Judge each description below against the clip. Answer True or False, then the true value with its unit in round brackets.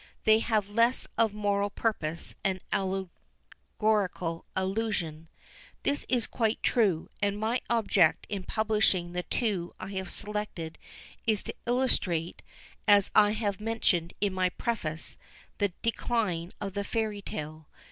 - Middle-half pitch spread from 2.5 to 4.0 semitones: True (3.4 semitones)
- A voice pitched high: True (205 Hz)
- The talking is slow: True (130 wpm)